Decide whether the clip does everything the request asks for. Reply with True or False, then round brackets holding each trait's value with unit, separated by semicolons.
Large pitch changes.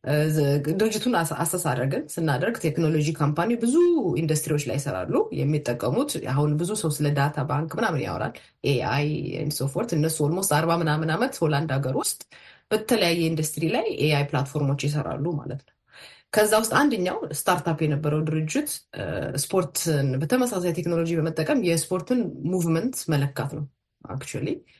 False (2.8 semitones)